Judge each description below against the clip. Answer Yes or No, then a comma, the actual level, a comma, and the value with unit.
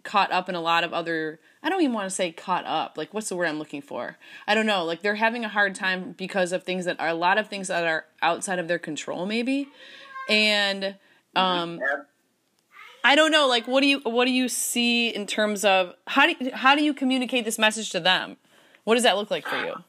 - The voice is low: No, high, 205 Hz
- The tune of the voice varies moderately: No, wide, 5.7 semitones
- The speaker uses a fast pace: Yes, fast, 245 wpm